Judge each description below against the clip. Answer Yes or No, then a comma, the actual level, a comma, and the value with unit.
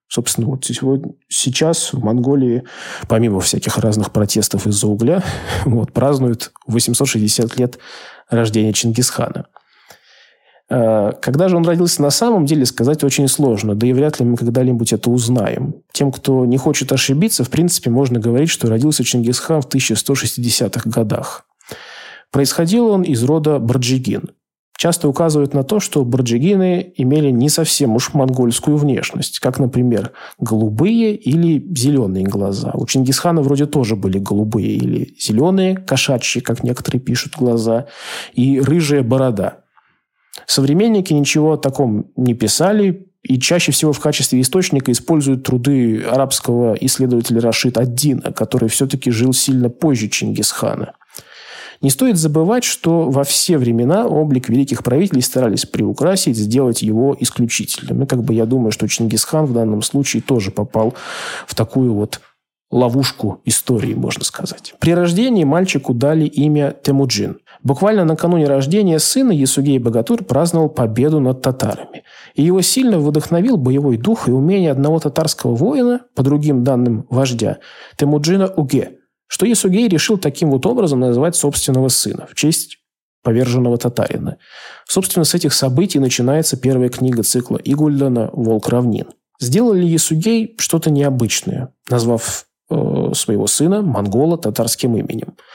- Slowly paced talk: No, average, 135 wpm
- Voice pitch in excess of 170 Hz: No, low, 135 Hz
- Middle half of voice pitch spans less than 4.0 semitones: No, average, 4.4 semitones